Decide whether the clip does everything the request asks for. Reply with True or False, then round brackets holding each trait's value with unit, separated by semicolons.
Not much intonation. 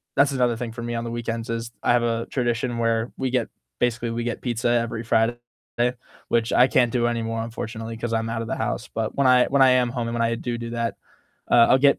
True (1.1 semitones)